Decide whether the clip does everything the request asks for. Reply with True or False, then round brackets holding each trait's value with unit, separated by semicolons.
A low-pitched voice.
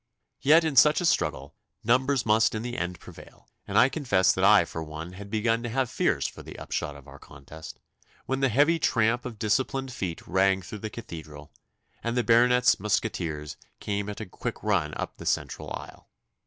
True (110 Hz)